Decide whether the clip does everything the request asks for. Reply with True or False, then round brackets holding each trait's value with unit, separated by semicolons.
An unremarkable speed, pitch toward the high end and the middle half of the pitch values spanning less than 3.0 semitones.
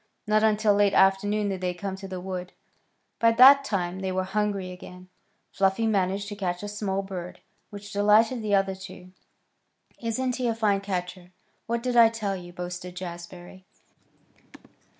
True (165 wpm; 195 Hz; 2.6 semitones)